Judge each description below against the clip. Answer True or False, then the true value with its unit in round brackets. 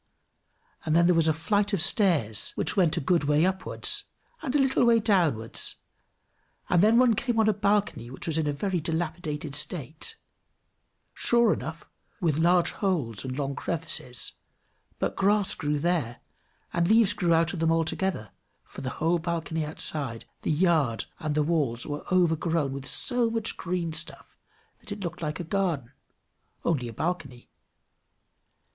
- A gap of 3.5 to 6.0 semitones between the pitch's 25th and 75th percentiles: True (4.4 semitones)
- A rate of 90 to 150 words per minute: False (160 wpm)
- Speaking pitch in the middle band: True (165 Hz)